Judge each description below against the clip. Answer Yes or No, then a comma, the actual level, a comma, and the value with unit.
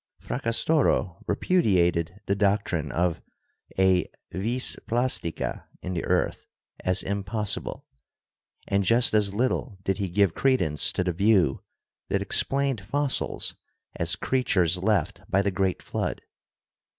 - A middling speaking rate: No, slow, 125 wpm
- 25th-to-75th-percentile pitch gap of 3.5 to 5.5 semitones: Yes, average, 4.3 semitones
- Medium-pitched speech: No, low, 100 Hz